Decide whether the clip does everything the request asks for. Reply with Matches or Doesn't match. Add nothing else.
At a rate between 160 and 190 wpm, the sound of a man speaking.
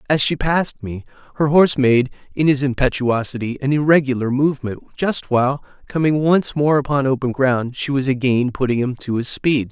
Matches